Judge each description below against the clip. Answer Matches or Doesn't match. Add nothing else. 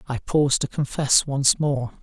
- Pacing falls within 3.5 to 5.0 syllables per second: Matches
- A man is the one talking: Matches